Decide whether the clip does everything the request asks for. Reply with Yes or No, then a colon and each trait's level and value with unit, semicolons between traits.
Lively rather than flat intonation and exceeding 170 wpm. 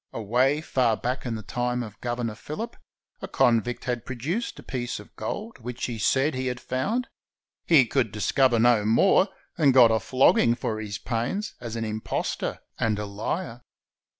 No: average, 2.8 semitones; average, 180 wpm